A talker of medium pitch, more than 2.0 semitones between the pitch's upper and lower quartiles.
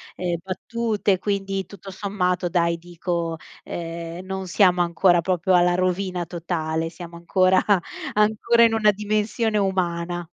Yes: medium, 180 Hz; narrow, 2.5 semitones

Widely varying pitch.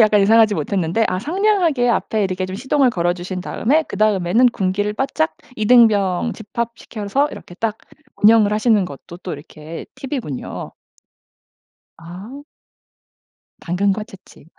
No: average, 4.5 semitones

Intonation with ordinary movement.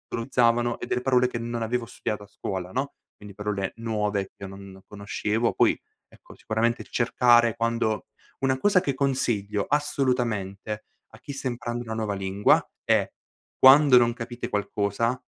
Yes: average, 3.3 semitones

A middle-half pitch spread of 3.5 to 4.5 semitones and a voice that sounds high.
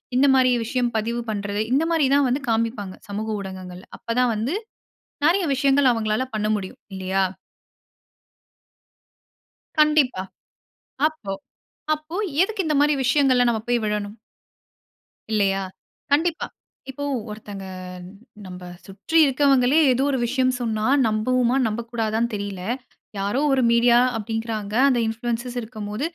Yes: average, 4.2 semitones; high, 235 Hz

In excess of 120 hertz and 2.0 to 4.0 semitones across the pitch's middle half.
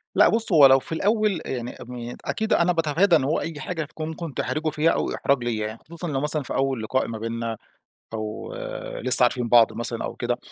No: low, 135 Hz; average, 5.2 semitones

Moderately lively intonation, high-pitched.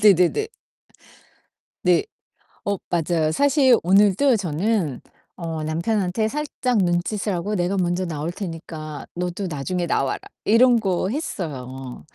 No: average, 4.7 semitones; medium, 180 Hz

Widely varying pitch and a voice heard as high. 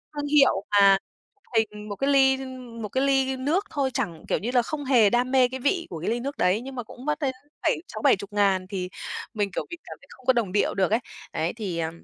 No: average, 4.8 semitones; high, 240 Hz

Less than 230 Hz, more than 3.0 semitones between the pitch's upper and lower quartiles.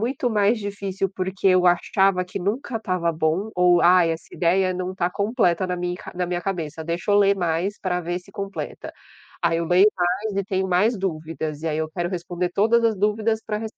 No: medium, 185 Hz; narrow, 2.4 semitones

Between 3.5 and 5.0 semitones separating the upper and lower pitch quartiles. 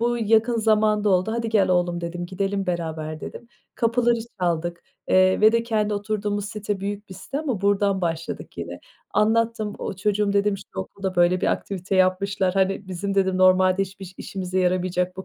No: narrow, 2.5 semitones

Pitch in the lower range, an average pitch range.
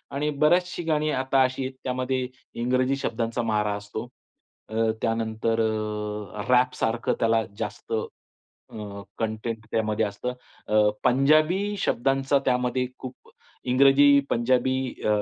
Yes: low, 125 Hz; average, 3.5 semitones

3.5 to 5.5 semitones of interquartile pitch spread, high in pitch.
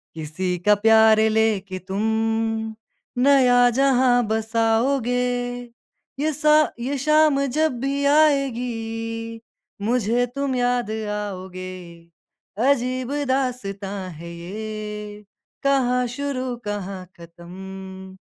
Yes: average, 4.0 semitones; high, 225 Hz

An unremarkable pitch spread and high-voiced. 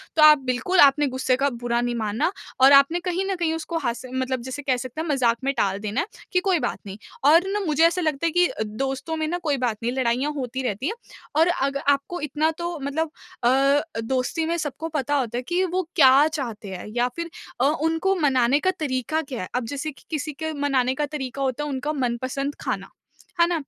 Yes: average, 3.9 semitones; very high, 280 Hz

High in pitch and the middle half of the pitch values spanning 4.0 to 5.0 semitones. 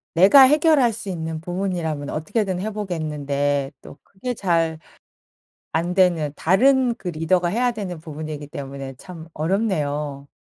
No: medium, 170 Hz; average, 4.7 semitones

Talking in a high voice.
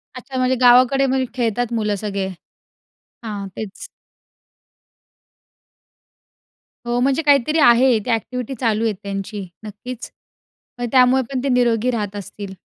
Yes: high, 240 Hz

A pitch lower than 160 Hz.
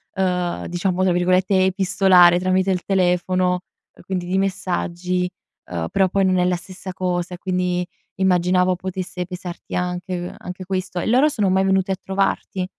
No: medium, 185 Hz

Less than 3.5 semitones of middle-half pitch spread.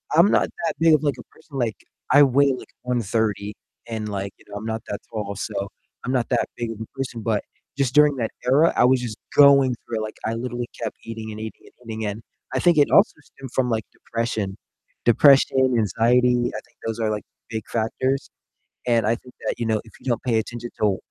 Yes: average, 3.0 semitones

